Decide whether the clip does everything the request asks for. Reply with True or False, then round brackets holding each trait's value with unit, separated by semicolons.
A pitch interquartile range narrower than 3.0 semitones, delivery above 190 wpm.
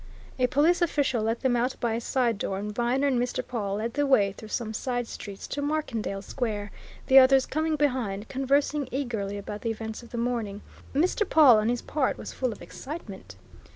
False (4.1 semitones; 200 wpm)